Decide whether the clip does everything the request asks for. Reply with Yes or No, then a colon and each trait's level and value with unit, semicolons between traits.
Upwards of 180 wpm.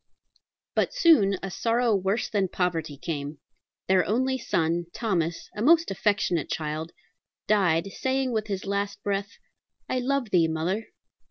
No: average, 140 wpm